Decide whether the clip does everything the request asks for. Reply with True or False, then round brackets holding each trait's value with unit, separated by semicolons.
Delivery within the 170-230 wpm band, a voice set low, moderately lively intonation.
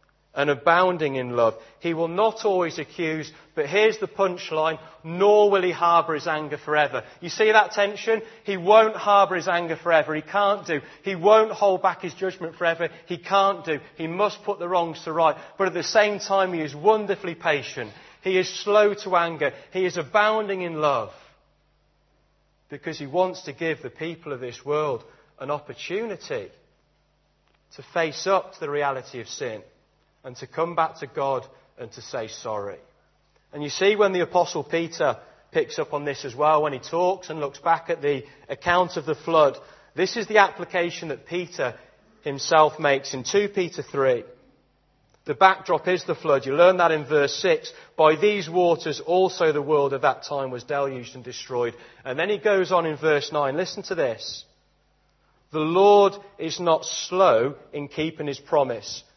False (185 wpm; 170 Hz; 4.3 semitones)